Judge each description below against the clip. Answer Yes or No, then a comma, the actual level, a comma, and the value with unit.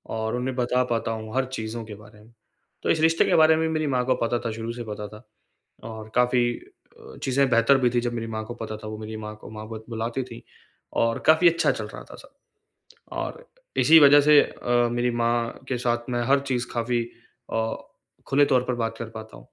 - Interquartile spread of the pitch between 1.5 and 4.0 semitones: Yes, average, 2.7 semitones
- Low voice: Yes, low, 120 Hz